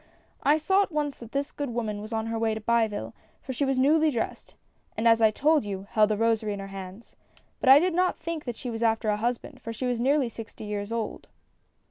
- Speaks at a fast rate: Yes, fast, 235 wpm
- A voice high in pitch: Yes, high, 230 Hz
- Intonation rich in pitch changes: No, average, 4.6 semitones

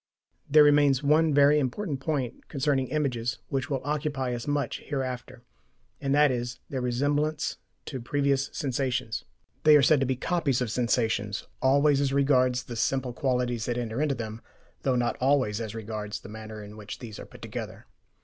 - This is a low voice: Yes, low, 130 Hz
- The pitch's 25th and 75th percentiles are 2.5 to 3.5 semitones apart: Yes, average, 3.1 semitones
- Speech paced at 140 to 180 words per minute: Yes, average, 175 wpm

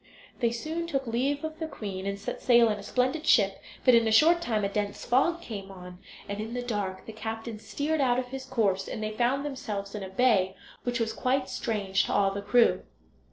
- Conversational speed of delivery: No, fast, 225 wpm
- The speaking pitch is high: Yes, high, 230 Hz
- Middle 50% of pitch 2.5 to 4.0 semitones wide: No, average, 4.4 semitones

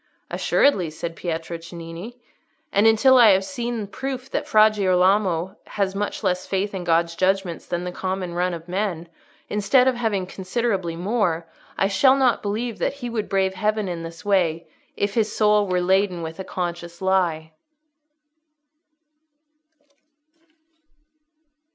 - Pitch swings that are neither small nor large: Yes, average, 3.6 semitones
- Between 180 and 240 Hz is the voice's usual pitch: Yes, high, 190 Hz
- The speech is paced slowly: No, average, 145 wpm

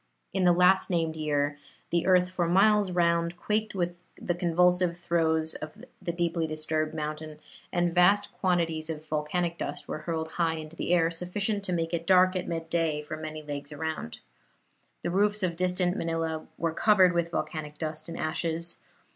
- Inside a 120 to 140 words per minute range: No, average, 170 wpm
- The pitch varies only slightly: Yes, narrow, 2.1 semitones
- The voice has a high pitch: No, medium, 170 Hz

